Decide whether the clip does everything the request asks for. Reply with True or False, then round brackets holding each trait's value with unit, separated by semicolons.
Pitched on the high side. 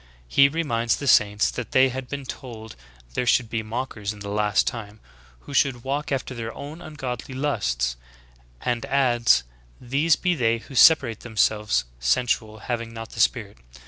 False (120 Hz)